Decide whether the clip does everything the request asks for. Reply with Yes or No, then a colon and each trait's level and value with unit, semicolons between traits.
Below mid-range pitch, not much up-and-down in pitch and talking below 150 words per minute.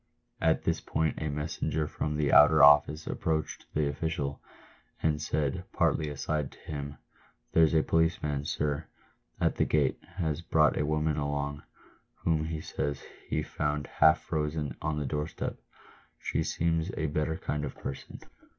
No: very low, 75 Hz; narrow, 1.4 semitones; average, 160 wpm